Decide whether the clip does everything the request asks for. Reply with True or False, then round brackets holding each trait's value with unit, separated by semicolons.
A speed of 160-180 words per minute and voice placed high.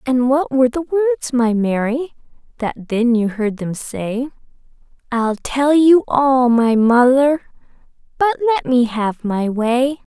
False (150 wpm; 255 Hz)